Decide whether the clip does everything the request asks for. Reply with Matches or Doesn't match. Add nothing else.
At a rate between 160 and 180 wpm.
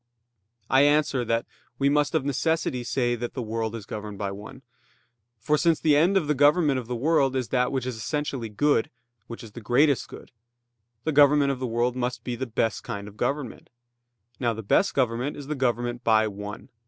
Doesn't match